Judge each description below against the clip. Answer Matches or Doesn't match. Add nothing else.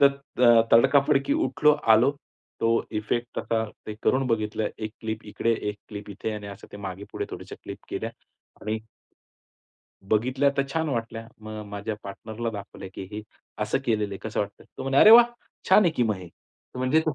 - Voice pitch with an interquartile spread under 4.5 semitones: Matches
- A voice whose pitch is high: Doesn't match